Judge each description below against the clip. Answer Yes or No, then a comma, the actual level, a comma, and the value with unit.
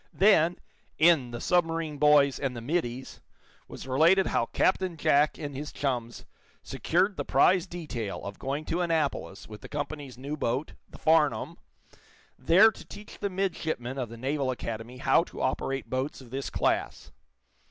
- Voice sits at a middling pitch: Yes, medium, 145 Hz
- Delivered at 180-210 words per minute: No, average, 160 wpm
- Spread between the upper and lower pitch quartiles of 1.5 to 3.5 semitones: No, average, 4.4 semitones